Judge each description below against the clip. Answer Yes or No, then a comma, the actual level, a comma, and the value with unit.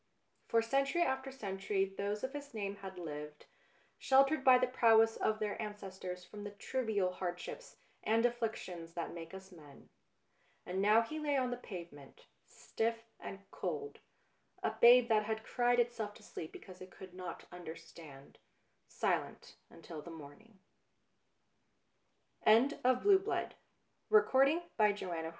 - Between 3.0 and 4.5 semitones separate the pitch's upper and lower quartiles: No, average, 5.0 semitones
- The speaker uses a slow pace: Yes, slow, 125 wpm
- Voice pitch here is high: Yes, high, 210 Hz